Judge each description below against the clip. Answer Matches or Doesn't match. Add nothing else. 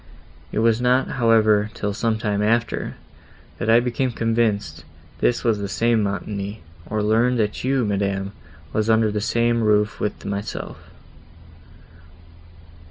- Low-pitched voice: Matches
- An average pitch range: Doesn't match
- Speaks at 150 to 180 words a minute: Doesn't match